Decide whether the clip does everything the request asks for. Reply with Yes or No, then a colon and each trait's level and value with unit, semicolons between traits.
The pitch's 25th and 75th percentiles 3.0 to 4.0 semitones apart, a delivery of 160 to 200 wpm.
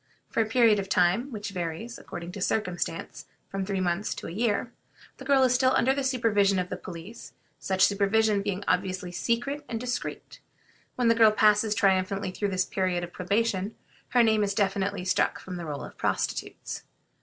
Yes: average, 3.6 semitones; average, 185 wpm